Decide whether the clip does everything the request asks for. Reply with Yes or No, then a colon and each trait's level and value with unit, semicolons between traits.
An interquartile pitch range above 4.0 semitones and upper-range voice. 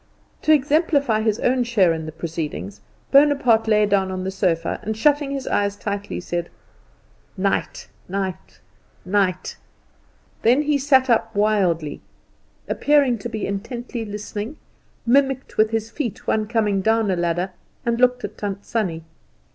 Yes: average, 4.6 semitones; high, 215 Hz